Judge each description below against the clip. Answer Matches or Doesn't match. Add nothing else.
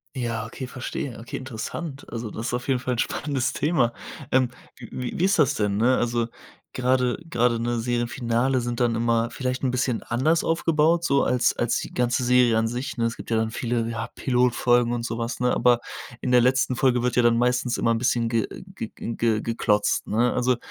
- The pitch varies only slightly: Matches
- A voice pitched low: Matches